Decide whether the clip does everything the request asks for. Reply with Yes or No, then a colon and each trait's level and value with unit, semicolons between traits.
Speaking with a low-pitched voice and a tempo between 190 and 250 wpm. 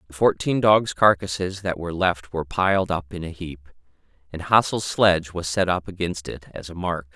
Yes: very low, 90 Hz; average, 200 wpm